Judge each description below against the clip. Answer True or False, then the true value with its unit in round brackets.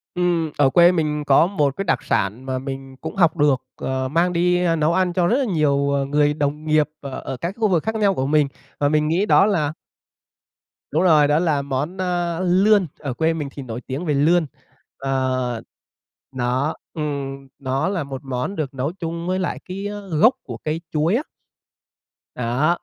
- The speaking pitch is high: False (155 Hz)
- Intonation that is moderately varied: True (4.4 semitones)